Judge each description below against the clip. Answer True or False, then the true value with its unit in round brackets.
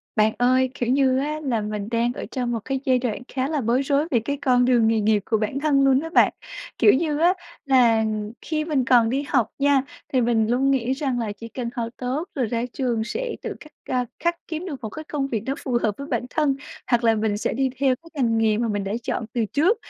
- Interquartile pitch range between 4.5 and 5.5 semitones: False (3.5 semitones)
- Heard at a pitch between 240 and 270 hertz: True (255 Hz)